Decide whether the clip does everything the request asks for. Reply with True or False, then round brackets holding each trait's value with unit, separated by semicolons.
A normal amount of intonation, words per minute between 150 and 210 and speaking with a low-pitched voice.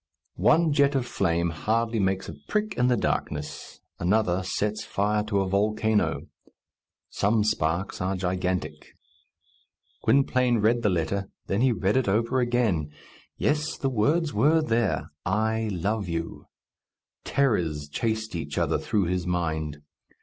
False (4.9 semitones; 135 wpm; 105 Hz)